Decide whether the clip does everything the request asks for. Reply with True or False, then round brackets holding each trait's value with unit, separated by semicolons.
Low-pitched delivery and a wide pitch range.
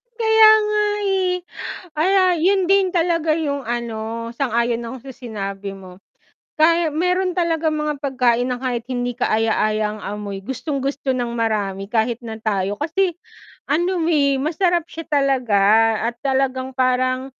False (265 Hz; 6.1 semitones)